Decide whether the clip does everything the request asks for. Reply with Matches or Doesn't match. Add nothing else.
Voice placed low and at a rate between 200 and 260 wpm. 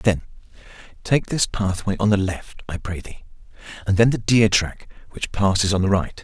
Doesn't match